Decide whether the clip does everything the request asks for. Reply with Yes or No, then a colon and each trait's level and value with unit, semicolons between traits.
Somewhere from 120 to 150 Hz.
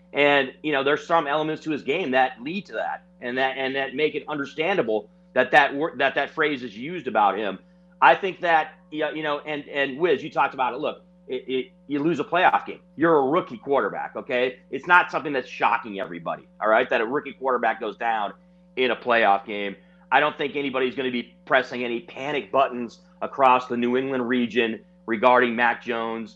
Yes: low, 135 Hz